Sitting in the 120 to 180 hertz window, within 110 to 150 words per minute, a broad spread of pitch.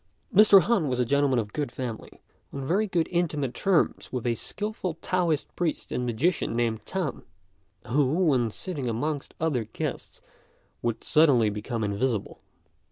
Yes: medium, 140 Hz; average, 145 wpm; wide, 6.3 semitones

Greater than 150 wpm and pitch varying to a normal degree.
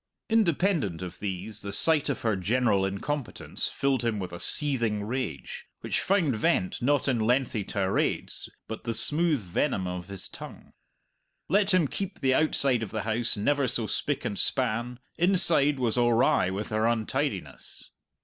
No: average, 160 wpm; wide, 5.9 semitones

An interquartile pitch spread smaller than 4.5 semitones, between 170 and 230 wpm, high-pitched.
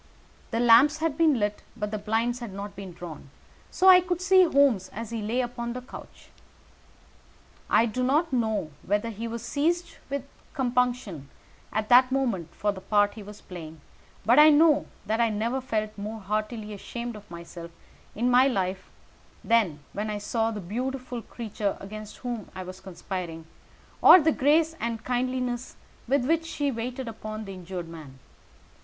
Yes: average, 4.0 semitones; average, 175 wpm; high, 230 Hz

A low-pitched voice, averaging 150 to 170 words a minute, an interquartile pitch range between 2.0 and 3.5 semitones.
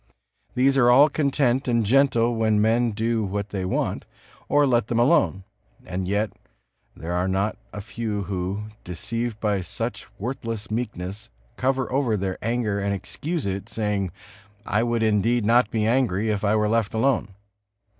Yes: low, 110 Hz; average, 160 wpm; average, 3.2 semitones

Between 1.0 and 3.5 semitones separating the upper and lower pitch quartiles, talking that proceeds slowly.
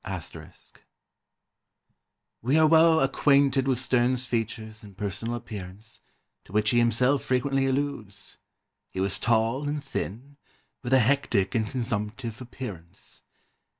No: average, 4.0 semitones; slow, 120 wpm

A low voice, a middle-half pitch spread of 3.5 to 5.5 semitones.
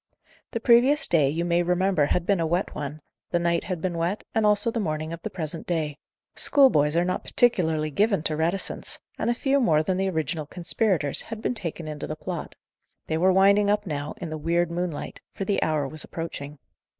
No: medium, 170 Hz; average, 4.1 semitones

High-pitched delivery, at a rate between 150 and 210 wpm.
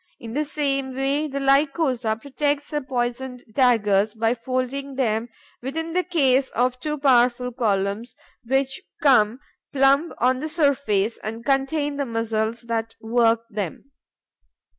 No: very high, 255 Hz; slow, 135 wpm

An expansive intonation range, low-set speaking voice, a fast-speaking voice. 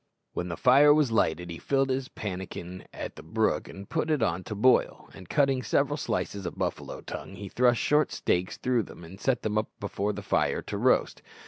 Yes: wide, 5.9 semitones; low, 105 Hz; fast, 210 wpm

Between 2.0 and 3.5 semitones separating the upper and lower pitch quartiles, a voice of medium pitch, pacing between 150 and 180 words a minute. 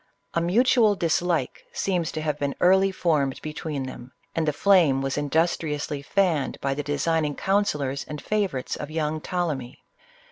No: average, 3.9 semitones; medium, 155 Hz; average, 165 wpm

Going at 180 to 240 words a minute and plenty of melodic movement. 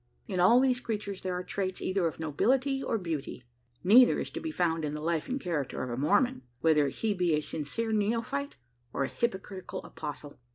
Yes: average, 200 wpm; wide, 6.7 semitones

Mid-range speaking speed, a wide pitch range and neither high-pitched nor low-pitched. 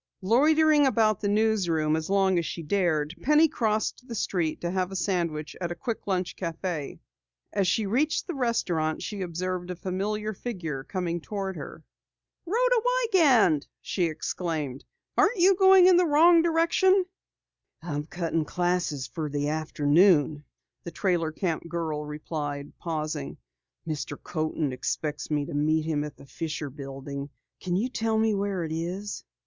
Yes: average, 155 wpm; wide, 5.9 semitones; medium, 180 Hz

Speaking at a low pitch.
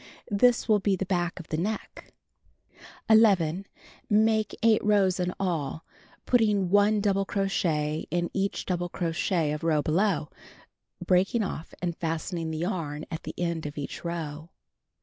No: medium, 180 Hz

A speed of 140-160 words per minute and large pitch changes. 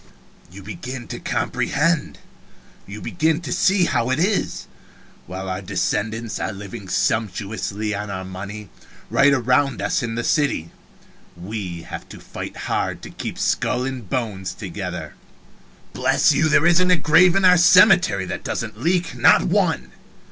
Yes: average, 150 wpm; wide, 8.4 semitones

